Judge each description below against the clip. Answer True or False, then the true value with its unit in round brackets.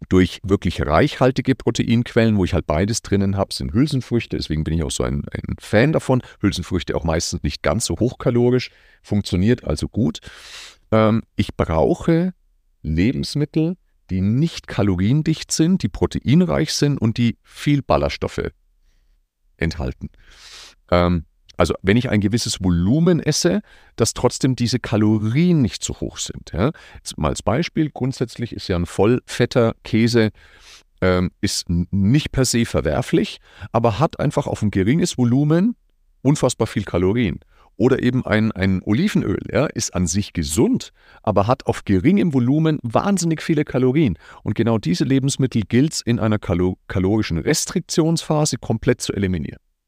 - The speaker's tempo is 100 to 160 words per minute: True (145 wpm)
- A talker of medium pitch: False (115 Hz)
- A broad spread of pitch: True (6.4 semitones)